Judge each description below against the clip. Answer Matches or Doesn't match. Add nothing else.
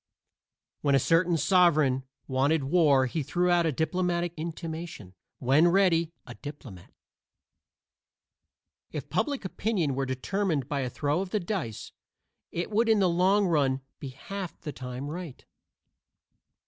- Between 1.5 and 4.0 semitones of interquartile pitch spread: Doesn't match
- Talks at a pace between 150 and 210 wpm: Doesn't match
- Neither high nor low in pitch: Matches